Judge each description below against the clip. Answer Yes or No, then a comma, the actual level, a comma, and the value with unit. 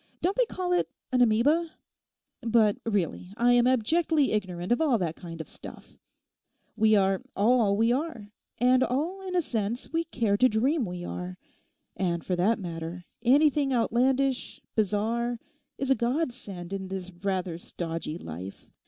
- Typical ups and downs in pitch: No, wide, 5.8 semitones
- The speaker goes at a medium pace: Yes, average, 155 wpm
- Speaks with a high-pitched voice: Yes, high, 225 Hz